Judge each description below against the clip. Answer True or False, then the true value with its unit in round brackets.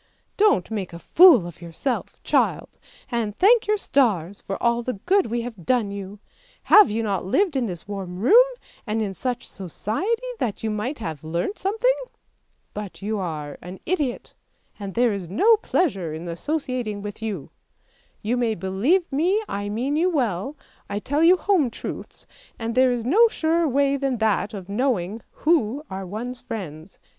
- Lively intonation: True (6.7 semitones)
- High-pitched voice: True (225 Hz)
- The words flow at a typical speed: True (170 wpm)